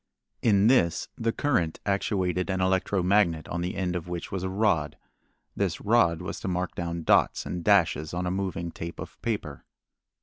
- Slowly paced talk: No, average, 180 wpm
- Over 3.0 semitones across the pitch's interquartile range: No, narrow, 2.6 semitones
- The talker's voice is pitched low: Yes, very low, 90 Hz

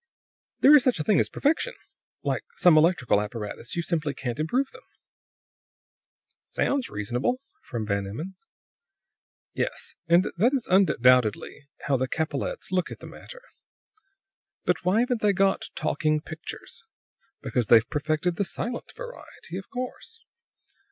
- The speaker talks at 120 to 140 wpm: Yes, slow, 135 wpm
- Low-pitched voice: No, medium, 170 Hz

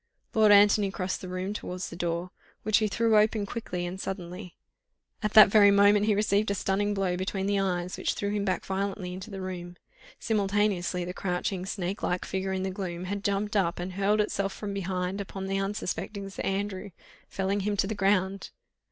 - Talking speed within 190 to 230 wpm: Yes, average, 195 wpm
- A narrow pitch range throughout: Yes, narrow, 1.9 semitones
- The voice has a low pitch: No, high, 195 Hz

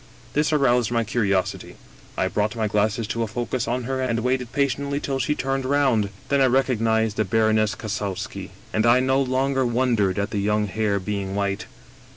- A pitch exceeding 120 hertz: No, low, 115 Hz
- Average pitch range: Yes, average, 3.7 semitones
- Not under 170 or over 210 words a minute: Yes, average, 190 wpm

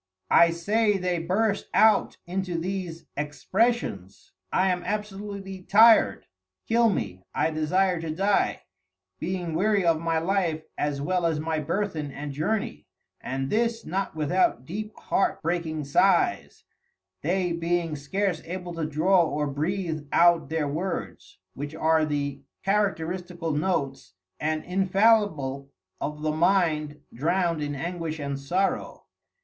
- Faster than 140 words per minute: No, slow, 135 wpm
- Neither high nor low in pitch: Yes, medium, 170 Hz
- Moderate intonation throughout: Yes, average, 4.1 semitones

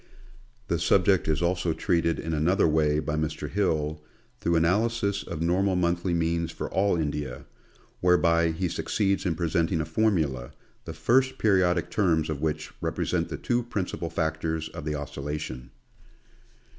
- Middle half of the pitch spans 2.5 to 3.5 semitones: Yes, average, 2.9 semitones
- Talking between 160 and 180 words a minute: No, average, 150 wpm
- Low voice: Yes, very low, 85 Hz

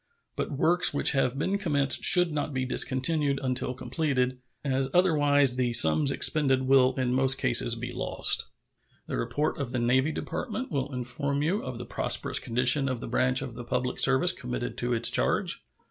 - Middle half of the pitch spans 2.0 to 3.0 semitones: Yes, narrow, 2.5 semitones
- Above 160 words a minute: Yes, average, 175 wpm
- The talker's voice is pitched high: No, low, 130 Hz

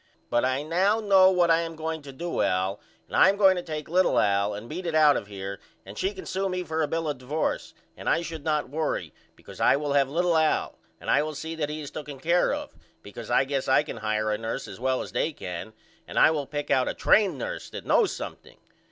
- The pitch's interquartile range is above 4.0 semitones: Yes, average, 4.6 semitones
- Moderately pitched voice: Yes, medium, 150 Hz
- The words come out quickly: Yes, fast, 255 wpm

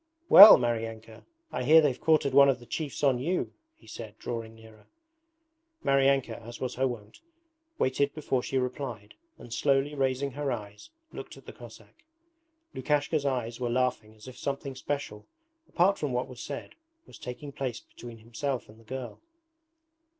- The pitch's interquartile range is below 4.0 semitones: Yes, average, 3.3 semitones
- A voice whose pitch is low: Yes, low, 130 Hz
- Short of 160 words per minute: No, average, 165 wpm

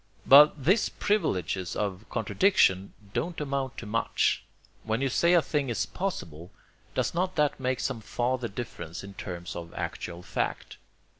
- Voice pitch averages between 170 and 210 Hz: No, low, 120 Hz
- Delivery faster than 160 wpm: No, average, 150 wpm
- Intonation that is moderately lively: No, wide, 7.8 semitones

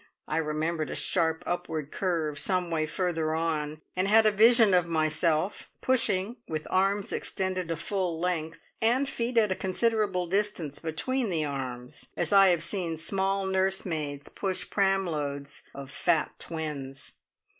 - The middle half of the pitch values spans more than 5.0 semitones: No, average, 3.9 semitones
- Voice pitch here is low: No, medium, 175 Hz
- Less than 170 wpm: Yes, average, 150 wpm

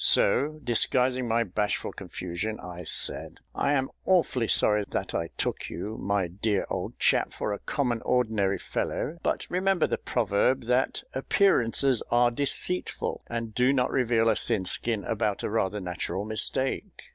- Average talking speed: Yes, average, 155 wpm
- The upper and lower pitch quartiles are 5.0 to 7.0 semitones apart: No, average, 4.1 semitones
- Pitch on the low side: Yes, low, 115 Hz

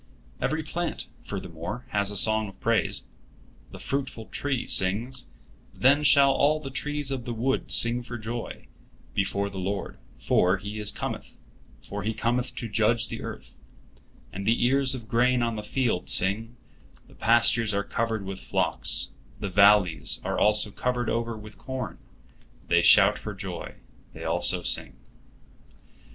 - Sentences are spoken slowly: No, average, 150 wpm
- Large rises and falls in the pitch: No, average, 3.7 semitones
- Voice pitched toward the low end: Yes, low, 115 Hz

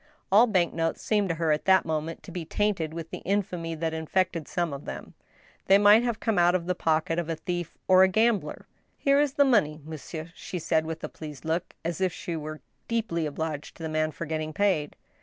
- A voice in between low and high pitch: Yes, medium, 170 Hz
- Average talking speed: No, fast, 230 wpm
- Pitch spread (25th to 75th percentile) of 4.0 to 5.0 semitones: No, average, 3.3 semitones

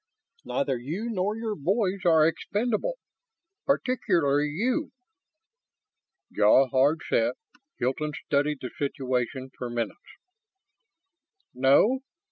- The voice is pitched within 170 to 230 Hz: No, medium, 150 Hz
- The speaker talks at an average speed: No, slow, 95 wpm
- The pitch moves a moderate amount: No, wide, 7.9 semitones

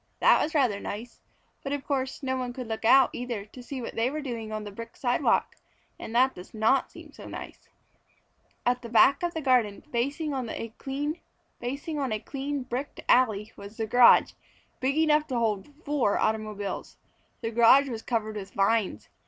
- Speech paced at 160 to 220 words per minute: Yes, average, 175 wpm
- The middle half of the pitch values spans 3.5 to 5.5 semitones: Yes, average, 3.8 semitones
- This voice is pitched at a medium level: No, high, 245 Hz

